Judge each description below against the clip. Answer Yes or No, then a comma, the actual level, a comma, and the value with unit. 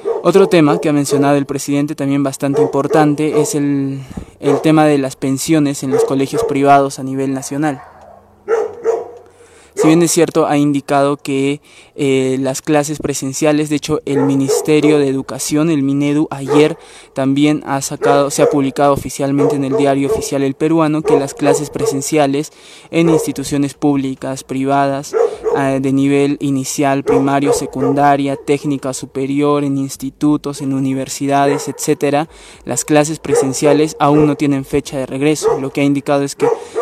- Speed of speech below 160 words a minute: Yes, average, 150 wpm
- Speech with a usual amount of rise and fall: No, narrow, 1.6 semitones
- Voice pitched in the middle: Yes, medium, 145 Hz